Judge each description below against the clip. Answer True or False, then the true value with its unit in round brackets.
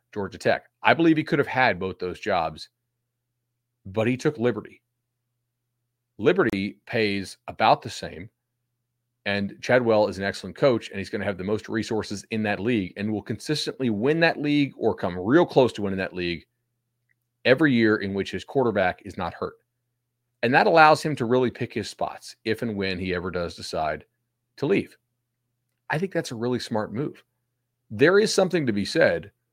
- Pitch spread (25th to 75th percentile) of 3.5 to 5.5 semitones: False (3.1 semitones)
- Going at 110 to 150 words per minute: False (185 wpm)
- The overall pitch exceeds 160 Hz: False (120 Hz)